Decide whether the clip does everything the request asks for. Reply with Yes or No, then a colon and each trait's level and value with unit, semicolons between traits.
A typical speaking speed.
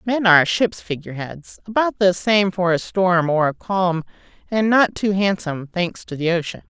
Yes: average, 195 wpm